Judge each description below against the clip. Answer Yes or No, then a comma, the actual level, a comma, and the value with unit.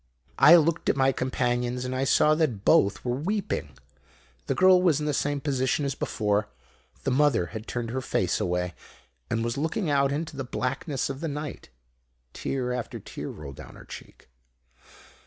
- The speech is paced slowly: No, average, 175 wpm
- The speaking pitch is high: No, low, 135 Hz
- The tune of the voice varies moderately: Yes, average, 3.5 semitones